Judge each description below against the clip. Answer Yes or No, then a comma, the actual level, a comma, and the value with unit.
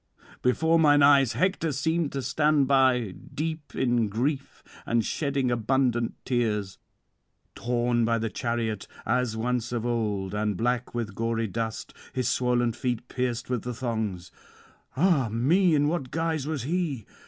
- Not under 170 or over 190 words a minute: No, average, 145 wpm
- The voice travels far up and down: No, average, 3.6 semitones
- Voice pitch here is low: Yes, low, 125 Hz